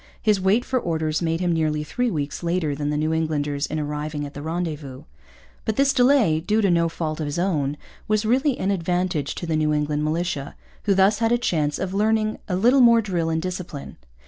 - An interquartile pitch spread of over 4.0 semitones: Yes, average, 5.3 semitones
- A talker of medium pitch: Yes, medium, 170 Hz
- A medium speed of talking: No, fast, 215 wpm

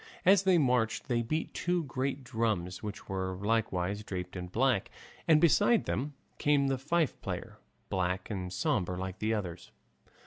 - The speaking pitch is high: No, low, 115 Hz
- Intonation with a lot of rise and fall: Yes, wide, 7.4 semitones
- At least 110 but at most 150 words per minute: No, average, 160 wpm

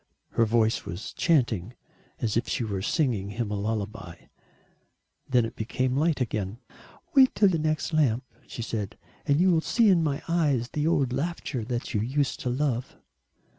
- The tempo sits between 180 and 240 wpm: No, average, 170 wpm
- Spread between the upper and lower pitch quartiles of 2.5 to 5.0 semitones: No, wide, 5.6 semitones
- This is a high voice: No, low, 125 Hz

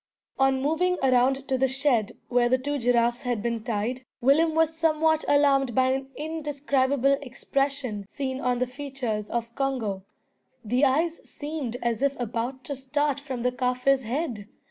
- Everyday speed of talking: Yes, average, 160 wpm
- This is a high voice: Yes, very high, 265 Hz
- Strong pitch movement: No, average, 2.7 semitones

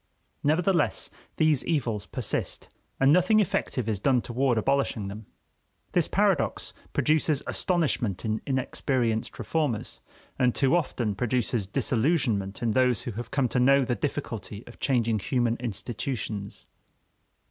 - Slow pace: Yes, slow, 125 wpm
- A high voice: No, low, 125 Hz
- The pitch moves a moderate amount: Yes, average, 4.0 semitones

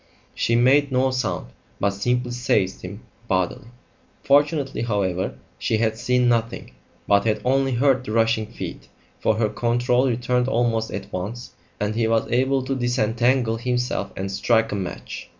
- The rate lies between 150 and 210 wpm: Yes, average, 155 wpm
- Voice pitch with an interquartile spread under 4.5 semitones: Yes, average, 2.8 semitones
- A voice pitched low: Yes, low, 120 Hz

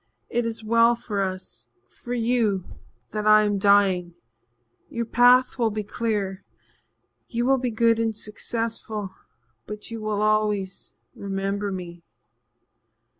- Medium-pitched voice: No, high, 215 Hz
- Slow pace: Yes, slow, 125 wpm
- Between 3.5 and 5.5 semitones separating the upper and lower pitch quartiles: No, narrow, 2.6 semitones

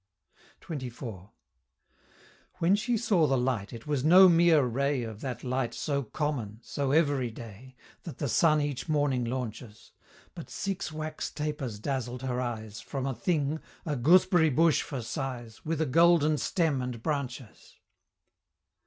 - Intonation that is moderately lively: Yes, average, 4.2 semitones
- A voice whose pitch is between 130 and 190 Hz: Yes, medium, 140 Hz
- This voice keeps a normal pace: Yes, average, 145 wpm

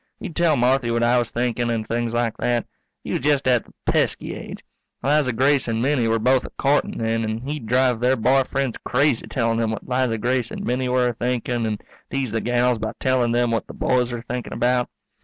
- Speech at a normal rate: No, fast, 225 wpm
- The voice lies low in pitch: Yes, low, 120 Hz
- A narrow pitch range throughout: Yes, narrow, 1.9 semitones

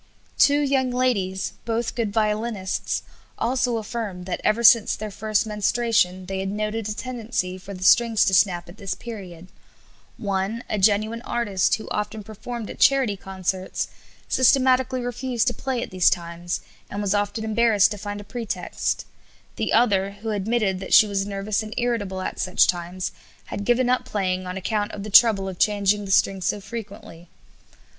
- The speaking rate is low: No, average, 170 wpm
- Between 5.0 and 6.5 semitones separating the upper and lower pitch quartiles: No, average, 3.4 semitones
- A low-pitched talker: No, high, 210 Hz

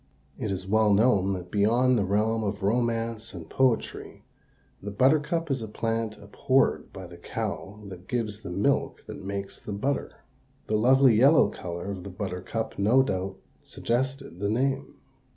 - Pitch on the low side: Yes, low, 110 Hz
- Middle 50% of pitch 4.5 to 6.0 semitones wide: No, average, 4.1 semitones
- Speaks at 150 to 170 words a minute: Yes, average, 160 wpm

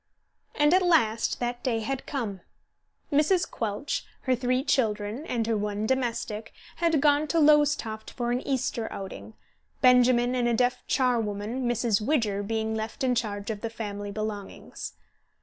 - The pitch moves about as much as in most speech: Yes, average, 3.4 semitones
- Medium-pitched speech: No, high, 240 Hz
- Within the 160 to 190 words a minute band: No, average, 150 wpm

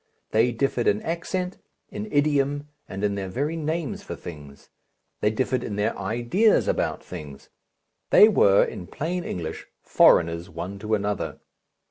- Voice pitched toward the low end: Yes, low, 115 Hz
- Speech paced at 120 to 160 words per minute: Yes, average, 145 wpm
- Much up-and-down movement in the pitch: Yes, wide, 8.2 semitones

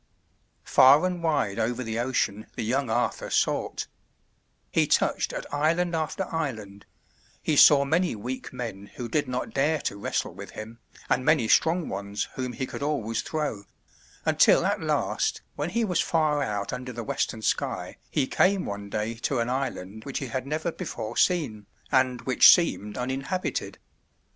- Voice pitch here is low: Yes, low, 130 Hz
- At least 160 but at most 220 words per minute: Yes, average, 165 wpm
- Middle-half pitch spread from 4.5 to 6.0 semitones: Yes, wide, 5.6 semitones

